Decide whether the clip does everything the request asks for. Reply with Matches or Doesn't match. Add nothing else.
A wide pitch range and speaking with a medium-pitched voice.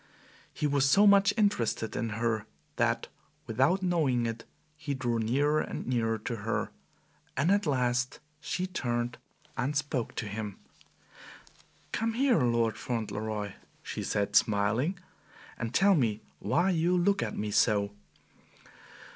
Doesn't match